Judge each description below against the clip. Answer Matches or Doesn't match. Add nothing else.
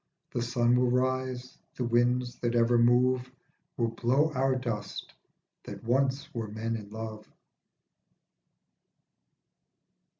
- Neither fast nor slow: Doesn't match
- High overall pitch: Doesn't match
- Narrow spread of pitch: Matches